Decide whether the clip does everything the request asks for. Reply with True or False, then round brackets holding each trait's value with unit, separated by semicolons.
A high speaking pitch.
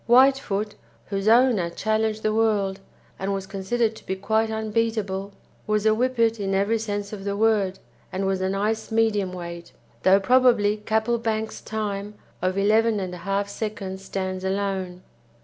True (205 Hz)